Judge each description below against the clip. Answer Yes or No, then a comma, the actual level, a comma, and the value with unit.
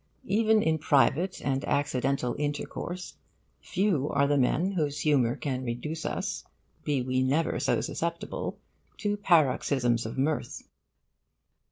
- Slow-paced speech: Yes, slow, 125 wpm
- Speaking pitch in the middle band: Yes, medium, 145 Hz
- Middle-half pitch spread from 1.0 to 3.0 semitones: No, average, 4.3 semitones